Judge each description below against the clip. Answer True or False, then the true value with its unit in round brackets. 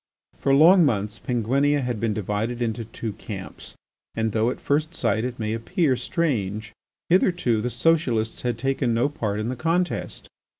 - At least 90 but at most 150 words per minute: False (165 wpm)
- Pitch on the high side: False (120 Hz)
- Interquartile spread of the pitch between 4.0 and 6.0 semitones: True (4.7 semitones)